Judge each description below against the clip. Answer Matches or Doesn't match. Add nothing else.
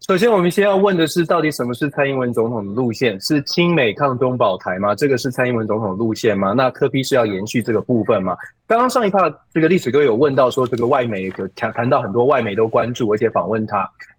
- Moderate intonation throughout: Doesn't match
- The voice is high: Doesn't match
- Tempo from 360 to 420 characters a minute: Matches